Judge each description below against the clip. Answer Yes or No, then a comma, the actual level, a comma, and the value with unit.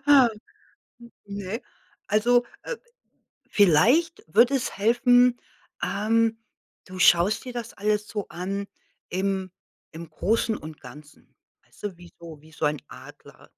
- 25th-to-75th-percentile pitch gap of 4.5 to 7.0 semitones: Yes, average, 5.0 semitones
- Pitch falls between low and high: No, high, 205 Hz